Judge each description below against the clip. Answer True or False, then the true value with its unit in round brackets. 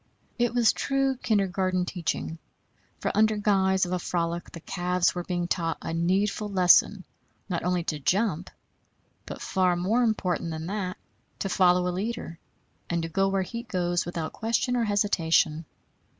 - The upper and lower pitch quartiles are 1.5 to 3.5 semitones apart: True (3.0 semitones)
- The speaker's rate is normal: True (160 wpm)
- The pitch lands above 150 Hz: True (185 Hz)